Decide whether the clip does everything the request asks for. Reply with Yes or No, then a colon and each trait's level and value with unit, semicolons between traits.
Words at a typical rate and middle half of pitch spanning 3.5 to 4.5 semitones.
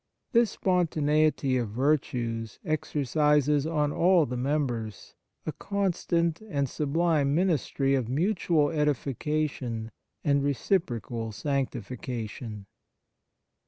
No: slow, 90 wpm; average, 4.0 semitones